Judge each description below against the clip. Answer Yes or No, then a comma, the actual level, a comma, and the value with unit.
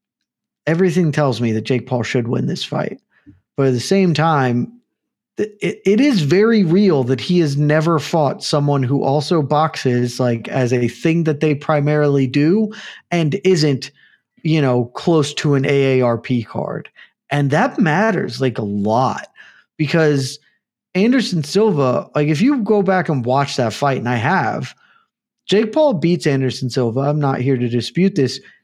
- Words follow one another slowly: No, average, 165 wpm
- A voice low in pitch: No, medium, 150 Hz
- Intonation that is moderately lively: No, wide, 5.7 semitones